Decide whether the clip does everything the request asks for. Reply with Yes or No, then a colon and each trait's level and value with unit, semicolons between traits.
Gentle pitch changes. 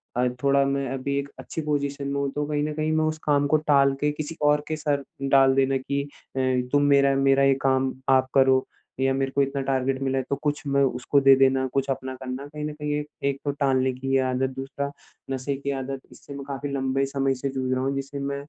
Yes: narrow, 1.2 semitones